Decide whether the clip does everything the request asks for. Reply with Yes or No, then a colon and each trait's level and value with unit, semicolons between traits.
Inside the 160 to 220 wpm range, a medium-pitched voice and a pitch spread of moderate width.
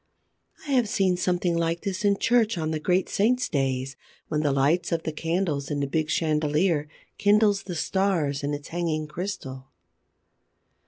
Yes: average, 165 wpm; medium, 165 Hz; average, 4.6 semitones